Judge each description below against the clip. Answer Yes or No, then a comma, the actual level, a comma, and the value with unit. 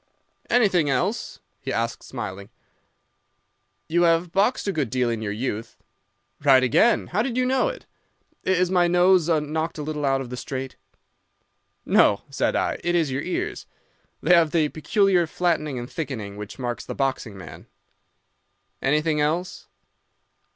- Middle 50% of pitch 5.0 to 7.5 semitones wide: Yes, wide, 5.5 semitones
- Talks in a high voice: No, medium, 155 Hz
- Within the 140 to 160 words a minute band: Yes, average, 150 wpm